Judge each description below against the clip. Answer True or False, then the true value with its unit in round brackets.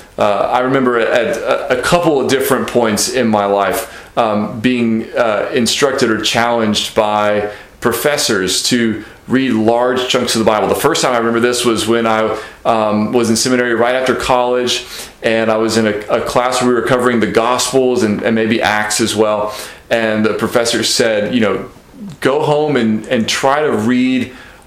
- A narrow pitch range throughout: True (2.3 semitones)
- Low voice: True (115 Hz)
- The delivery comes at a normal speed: True (180 wpm)